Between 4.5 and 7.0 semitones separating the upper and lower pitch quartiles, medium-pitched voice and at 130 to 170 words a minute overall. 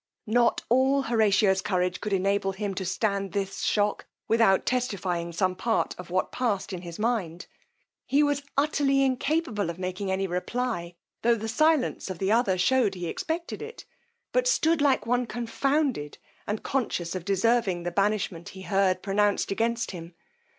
No: average, 4.9 semitones; high, 205 Hz; average, 160 wpm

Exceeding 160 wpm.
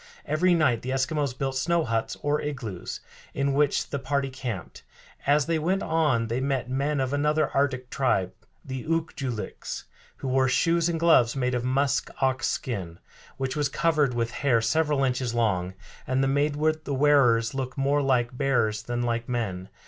Yes: average, 175 wpm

